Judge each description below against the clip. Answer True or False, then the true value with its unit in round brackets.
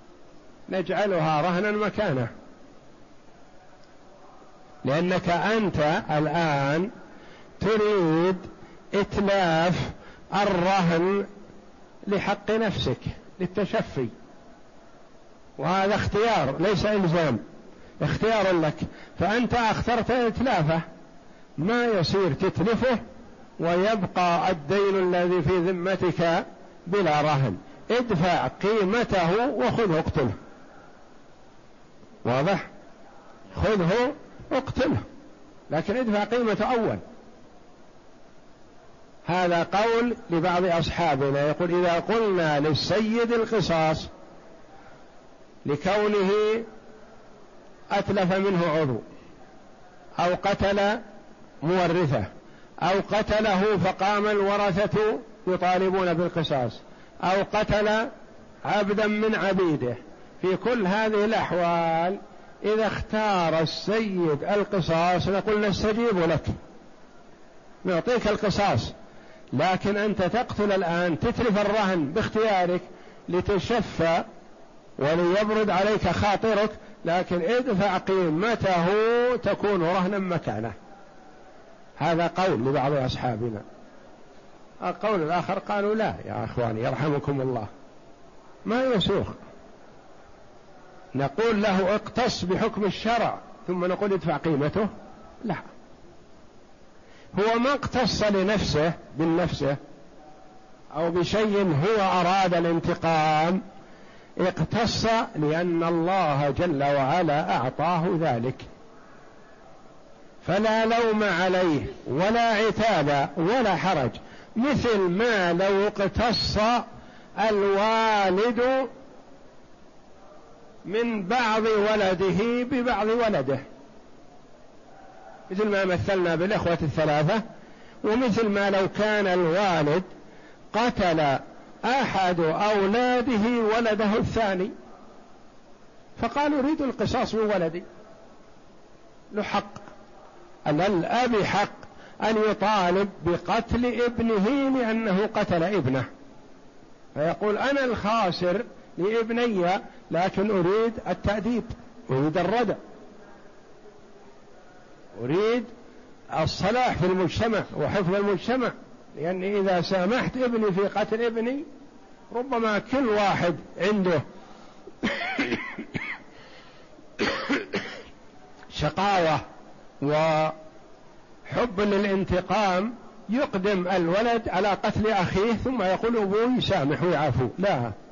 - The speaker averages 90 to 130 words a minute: False (75 wpm)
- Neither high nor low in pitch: False (195 Hz)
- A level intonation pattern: False (4.0 semitones)